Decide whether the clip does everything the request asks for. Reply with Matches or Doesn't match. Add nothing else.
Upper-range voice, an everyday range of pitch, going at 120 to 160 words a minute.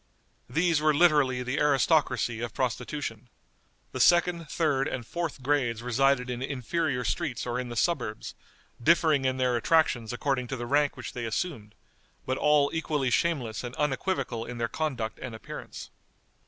Doesn't match